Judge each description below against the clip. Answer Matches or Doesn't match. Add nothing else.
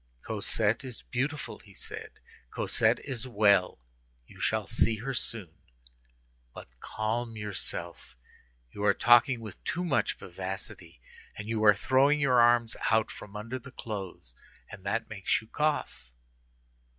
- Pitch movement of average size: Matches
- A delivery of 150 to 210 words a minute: Doesn't match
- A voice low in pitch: Matches